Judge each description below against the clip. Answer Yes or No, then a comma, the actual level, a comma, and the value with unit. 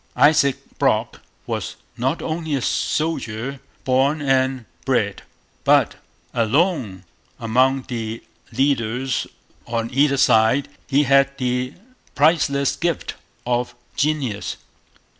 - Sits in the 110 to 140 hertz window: Yes, low, 135 Hz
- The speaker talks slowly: Yes, slow, 100 wpm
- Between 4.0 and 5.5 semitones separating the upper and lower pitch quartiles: No, average, 2.9 semitones